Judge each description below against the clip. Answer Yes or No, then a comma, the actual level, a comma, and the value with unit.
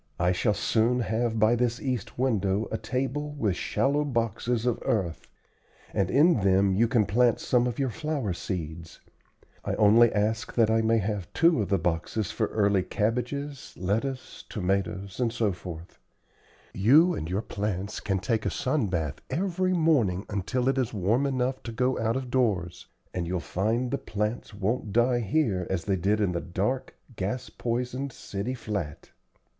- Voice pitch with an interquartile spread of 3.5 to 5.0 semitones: Yes, average, 4.4 semitones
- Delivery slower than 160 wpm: No, average, 165 wpm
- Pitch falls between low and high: No, low, 110 Hz